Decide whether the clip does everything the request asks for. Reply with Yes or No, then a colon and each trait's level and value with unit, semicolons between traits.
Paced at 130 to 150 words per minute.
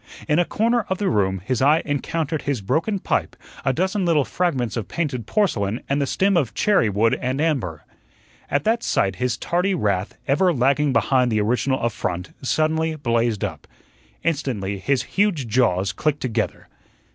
No: average, 170 wpm